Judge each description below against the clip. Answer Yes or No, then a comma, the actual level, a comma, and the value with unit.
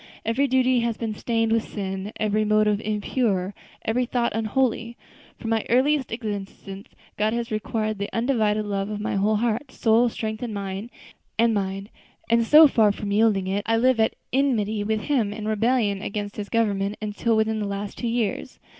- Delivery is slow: No, average, 170 wpm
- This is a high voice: Yes, high, 220 Hz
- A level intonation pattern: Yes, narrow, 2.2 semitones